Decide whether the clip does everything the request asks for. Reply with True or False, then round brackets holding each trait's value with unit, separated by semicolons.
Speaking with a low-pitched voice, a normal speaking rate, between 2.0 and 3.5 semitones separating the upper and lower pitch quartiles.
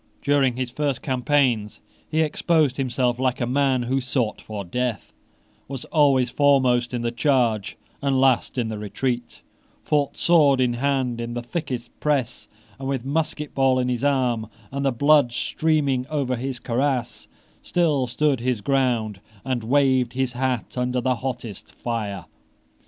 True (130 Hz; 155 wpm; 2.4 semitones)